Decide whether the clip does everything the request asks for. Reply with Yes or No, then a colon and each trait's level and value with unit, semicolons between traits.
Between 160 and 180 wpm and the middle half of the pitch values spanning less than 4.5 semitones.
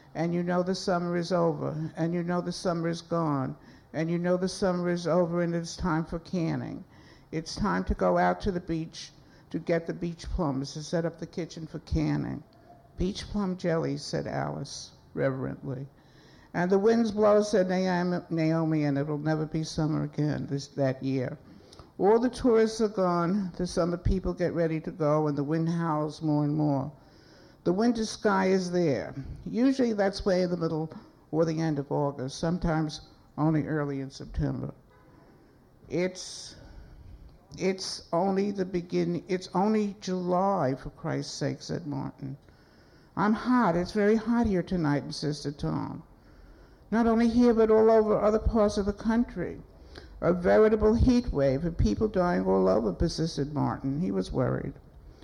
Yes: average, 165 wpm; average, 4.1 semitones